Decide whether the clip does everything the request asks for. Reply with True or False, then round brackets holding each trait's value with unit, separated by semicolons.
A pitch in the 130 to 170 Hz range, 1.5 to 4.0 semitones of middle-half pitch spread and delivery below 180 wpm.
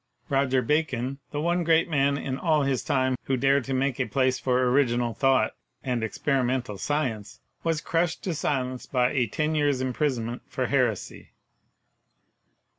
True (135 Hz; 2.8 semitones; 155 wpm)